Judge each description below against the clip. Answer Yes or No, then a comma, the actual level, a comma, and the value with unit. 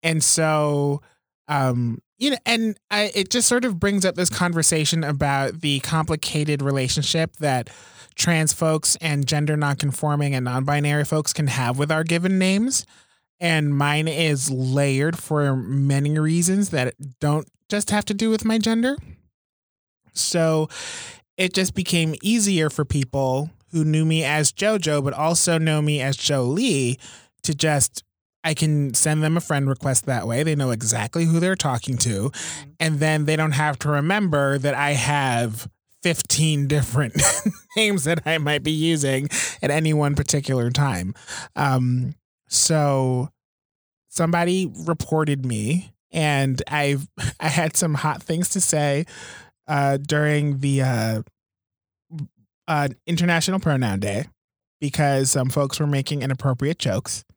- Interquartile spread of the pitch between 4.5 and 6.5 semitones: No, average, 3.2 semitones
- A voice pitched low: No, medium, 150 Hz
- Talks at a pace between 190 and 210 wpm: No, average, 145 wpm